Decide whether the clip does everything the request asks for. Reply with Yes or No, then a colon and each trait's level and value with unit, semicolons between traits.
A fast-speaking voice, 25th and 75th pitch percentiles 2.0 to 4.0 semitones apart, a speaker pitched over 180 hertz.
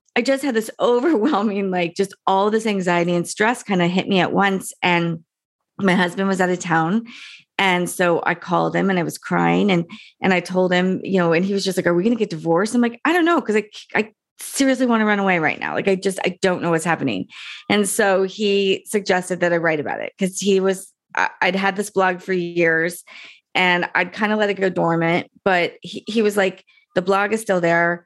Yes: fast, 235 wpm; average, 2.9 semitones; high, 190 Hz